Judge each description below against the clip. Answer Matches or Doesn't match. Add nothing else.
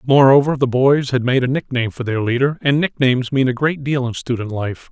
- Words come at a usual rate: Doesn't match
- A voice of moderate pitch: Doesn't match